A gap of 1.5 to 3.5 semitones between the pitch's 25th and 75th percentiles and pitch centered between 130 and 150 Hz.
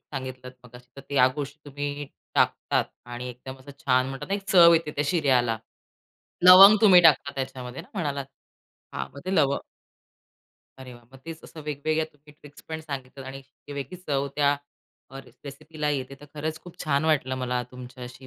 Yes: average, 3.1 semitones; medium, 140 Hz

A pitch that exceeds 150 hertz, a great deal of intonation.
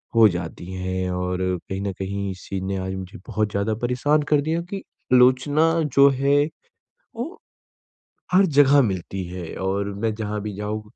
No: low, 105 Hz; wide, 6.5 semitones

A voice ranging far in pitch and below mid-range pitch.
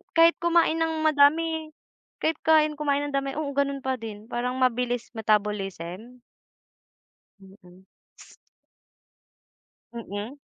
No: wide, 6.1 semitones; very high, 265 Hz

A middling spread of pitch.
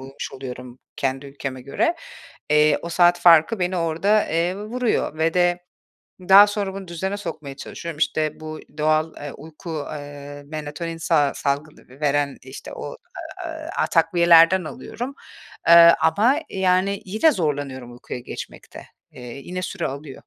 Yes: average, 4.2 semitones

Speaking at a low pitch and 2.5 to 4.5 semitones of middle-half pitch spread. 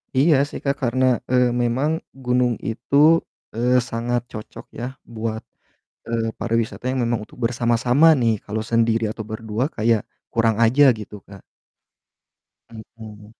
No: low, 115 Hz; narrow, 1.9 semitones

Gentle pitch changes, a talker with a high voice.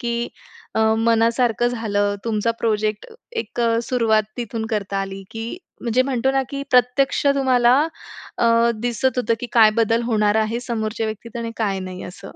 Yes: narrow, 2.1 semitones; high, 230 Hz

